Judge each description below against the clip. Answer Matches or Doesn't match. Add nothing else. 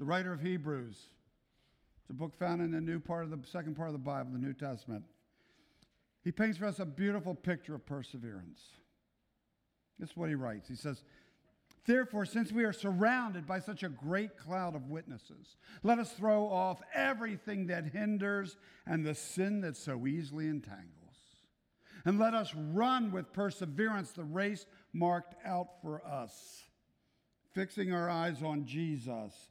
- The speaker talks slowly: Doesn't match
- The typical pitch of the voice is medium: Matches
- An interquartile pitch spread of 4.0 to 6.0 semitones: Matches